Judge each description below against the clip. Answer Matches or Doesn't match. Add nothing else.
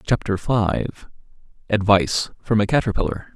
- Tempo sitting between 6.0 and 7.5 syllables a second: Doesn't match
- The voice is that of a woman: Doesn't match